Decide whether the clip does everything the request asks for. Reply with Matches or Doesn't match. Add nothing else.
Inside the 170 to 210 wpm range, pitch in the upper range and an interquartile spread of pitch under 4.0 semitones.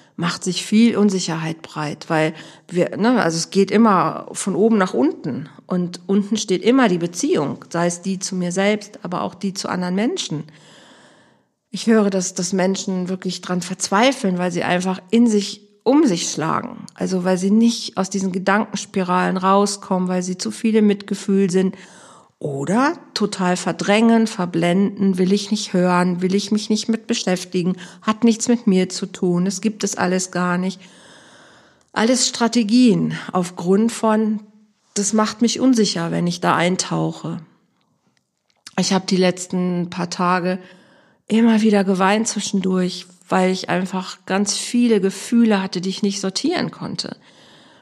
Doesn't match